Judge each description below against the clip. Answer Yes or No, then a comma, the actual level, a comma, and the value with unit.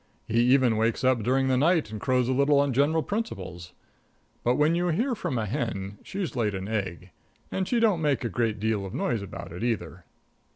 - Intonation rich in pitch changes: Yes, wide, 6.1 semitones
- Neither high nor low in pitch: No, low, 125 Hz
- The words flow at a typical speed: No, fast, 210 wpm